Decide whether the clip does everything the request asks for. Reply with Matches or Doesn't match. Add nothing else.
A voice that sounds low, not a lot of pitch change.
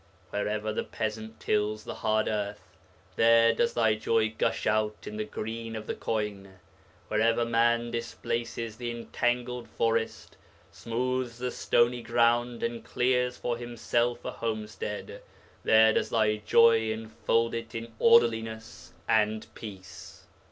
Matches